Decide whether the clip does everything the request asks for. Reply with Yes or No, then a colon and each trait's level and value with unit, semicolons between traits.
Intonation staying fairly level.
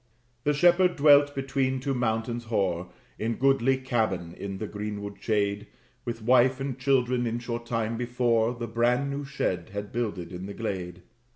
No: average, 4.1 semitones